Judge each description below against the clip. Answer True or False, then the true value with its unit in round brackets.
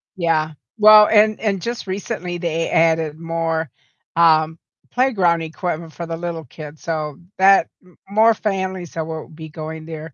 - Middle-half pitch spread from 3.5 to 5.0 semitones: False (3.0 semitones)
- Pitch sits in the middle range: True (165 Hz)